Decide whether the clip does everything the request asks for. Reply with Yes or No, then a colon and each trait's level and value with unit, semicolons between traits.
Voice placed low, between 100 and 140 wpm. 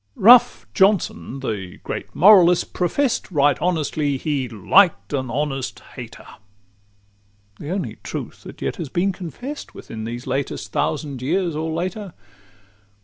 No: medium, 155 Hz; slow, 135 wpm